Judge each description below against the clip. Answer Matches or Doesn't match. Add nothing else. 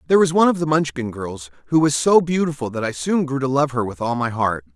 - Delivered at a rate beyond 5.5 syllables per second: Matches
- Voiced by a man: Matches